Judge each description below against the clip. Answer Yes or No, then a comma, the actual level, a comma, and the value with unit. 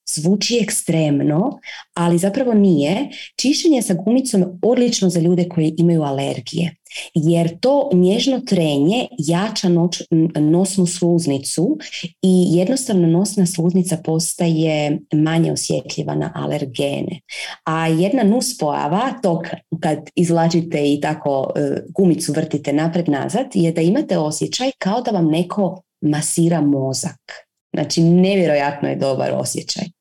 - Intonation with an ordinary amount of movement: Yes, average, 3.3 semitones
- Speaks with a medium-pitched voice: Yes, medium, 170 Hz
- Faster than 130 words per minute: No, average, 115 wpm